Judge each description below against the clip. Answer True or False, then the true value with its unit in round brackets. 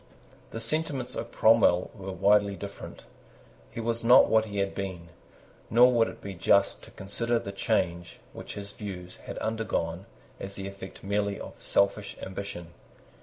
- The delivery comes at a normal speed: True (160 wpm)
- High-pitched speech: False (100 Hz)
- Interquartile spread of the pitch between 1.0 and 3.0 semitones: True (2.7 semitones)